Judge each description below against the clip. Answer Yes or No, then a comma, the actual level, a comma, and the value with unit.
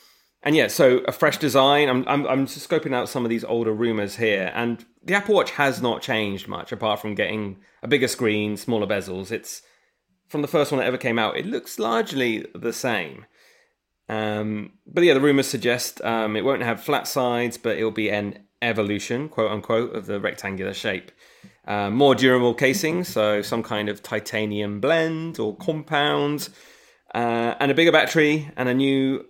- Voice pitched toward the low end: Yes, low, 120 Hz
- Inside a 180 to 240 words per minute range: Yes, average, 185 wpm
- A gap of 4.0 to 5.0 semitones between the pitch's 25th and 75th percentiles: Yes, average, 4.4 semitones